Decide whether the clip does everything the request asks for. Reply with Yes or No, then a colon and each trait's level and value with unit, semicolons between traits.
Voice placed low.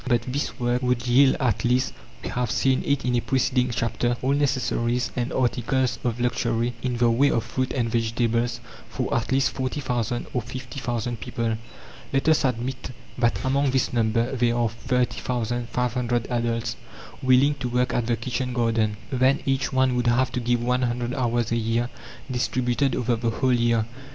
Yes: low, 120 Hz